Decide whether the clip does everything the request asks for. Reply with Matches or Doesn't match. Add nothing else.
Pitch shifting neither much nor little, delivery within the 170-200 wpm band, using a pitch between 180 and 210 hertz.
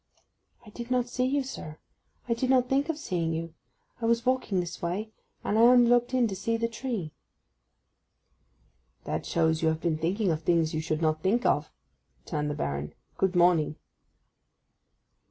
Doesn't match